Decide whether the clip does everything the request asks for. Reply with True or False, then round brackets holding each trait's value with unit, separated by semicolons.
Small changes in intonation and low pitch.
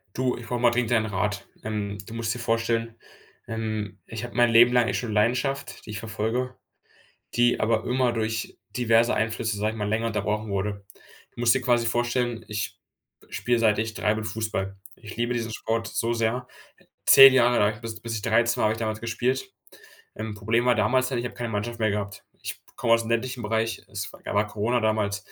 True (1.9 semitones; 115 Hz)